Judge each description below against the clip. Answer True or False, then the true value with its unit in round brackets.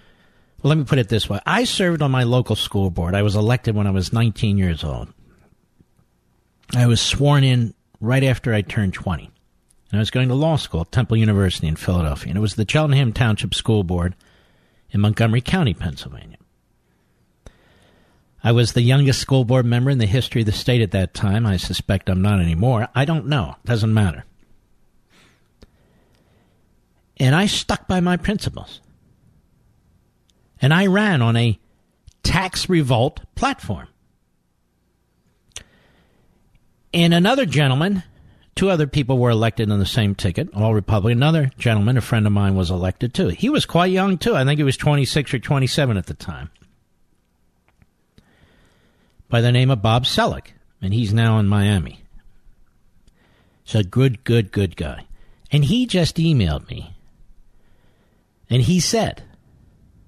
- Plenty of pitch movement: True (6.0 semitones)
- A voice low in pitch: True (115 Hz)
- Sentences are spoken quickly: False (160 wpm)